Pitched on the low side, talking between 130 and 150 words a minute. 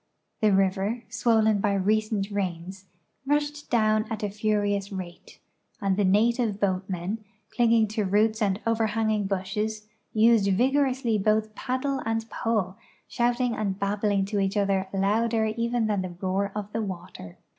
No: high, 210 Hz; average, 145 wpm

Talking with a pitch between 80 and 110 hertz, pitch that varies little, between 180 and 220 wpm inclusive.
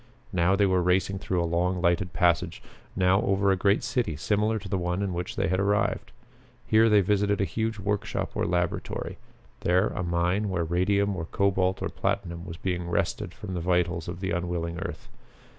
Yes: very low, 95 Hz; narrow, 2.3 semitones; average, 190 wpm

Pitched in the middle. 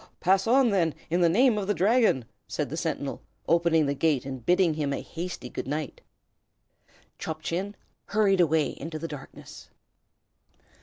Yes: medium, 170 Hz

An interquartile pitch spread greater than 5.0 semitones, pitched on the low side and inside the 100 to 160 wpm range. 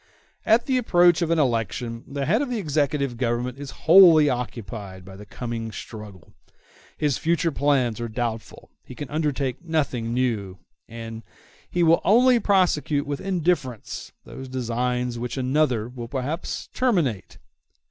Yes: wide, 5.5 semitones; low, 130 Hz; average, 145 wpm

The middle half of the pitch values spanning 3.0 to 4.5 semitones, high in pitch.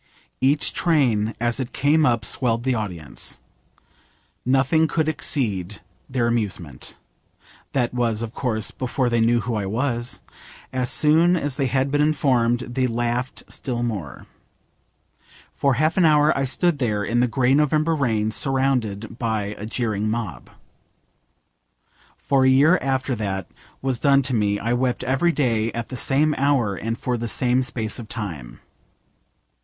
No: average, 3.5 semitones; low, 125 Hz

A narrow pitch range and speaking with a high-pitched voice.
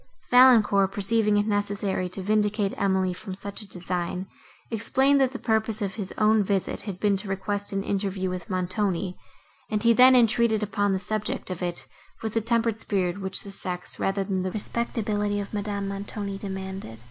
Yes: narrow, 2.1 semitones; high, 200 Hz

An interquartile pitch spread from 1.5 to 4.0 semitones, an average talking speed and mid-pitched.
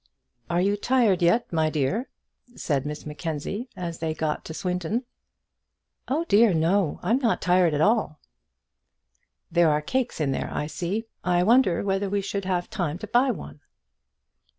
No: average, 5.2 semitones; average, 160 wpm; medium, 180 Hz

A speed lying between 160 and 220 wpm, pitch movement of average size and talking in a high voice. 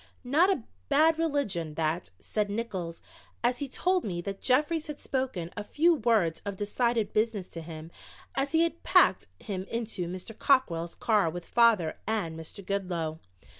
No: average, 165 wpm; wide, 7.3 semitones; high, 210 Hz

